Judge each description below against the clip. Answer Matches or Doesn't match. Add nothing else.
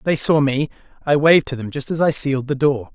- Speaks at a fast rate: Matches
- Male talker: Matches